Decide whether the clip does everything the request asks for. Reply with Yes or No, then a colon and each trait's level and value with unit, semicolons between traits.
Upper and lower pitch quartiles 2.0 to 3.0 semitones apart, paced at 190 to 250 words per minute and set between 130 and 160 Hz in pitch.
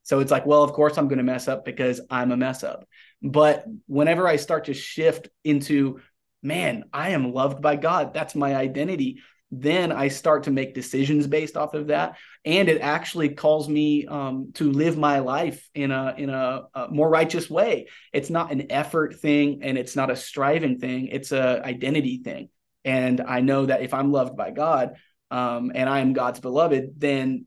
Yes: narrow, 2.5 semitones; average, 200 wpm; medium, 140 Hz